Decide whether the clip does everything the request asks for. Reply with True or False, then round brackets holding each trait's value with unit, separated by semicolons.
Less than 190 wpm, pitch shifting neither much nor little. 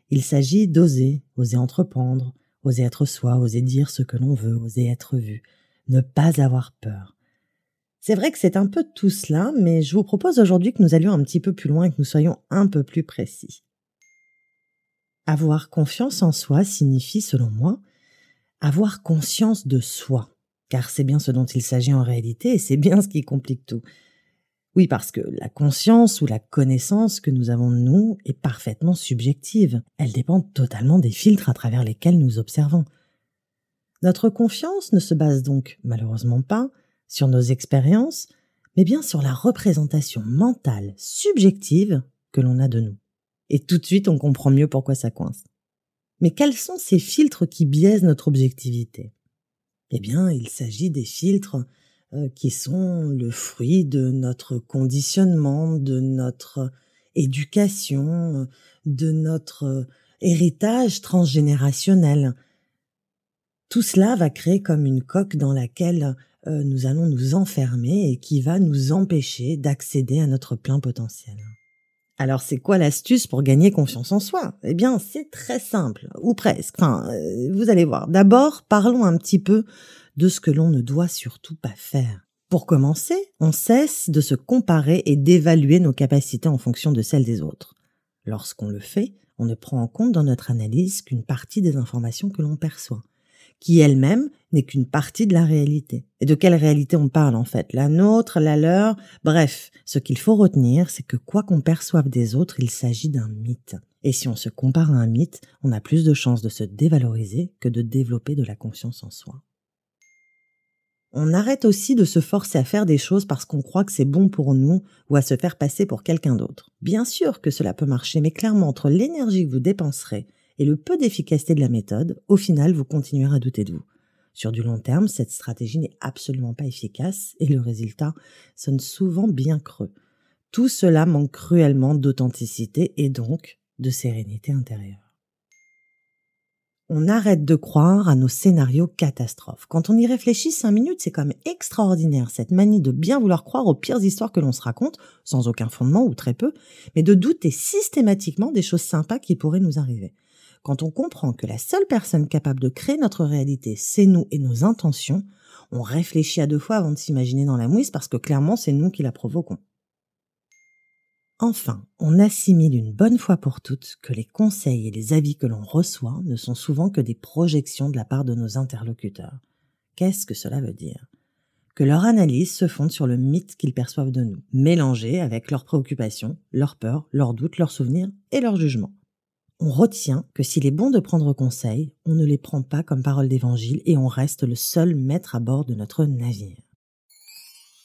False (180 wpm; 5.9 semitones)